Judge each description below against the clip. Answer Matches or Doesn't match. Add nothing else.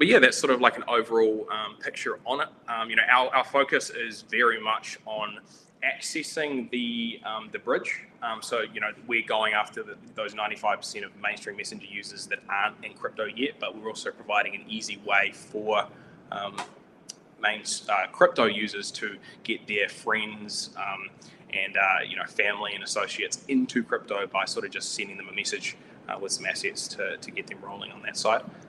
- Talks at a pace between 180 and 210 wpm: Matches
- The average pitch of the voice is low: Matches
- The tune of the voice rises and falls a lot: Matches